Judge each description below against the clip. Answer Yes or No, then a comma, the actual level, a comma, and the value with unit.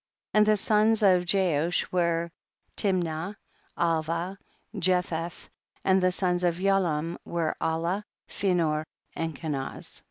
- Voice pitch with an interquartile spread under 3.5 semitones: Yes, narrow, 2.5 semitones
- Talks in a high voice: No, medium, 175 Hz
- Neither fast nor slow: No, slow, 120 wpm